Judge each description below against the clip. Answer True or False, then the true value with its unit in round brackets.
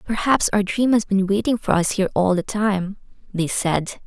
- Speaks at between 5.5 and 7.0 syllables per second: False (5.0 syllables/s)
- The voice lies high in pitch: True (200 Hz)